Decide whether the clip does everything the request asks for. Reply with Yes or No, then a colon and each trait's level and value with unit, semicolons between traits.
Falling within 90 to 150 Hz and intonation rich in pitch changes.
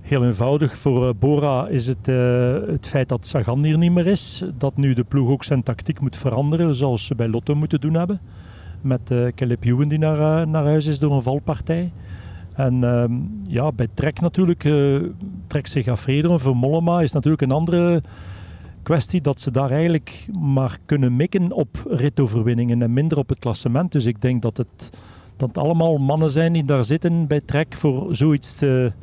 No: medium, 140 Hz; average, 3.8 semitones